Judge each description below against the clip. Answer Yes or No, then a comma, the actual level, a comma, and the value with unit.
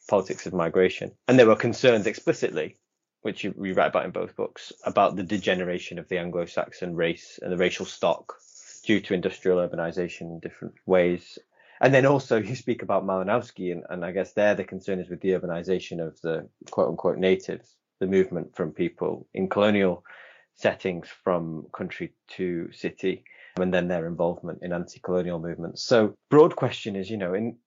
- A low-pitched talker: Yes, very low, 95 Hz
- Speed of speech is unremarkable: Yes, average, 180 wpm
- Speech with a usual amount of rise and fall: No, narrow, 1.5 semitones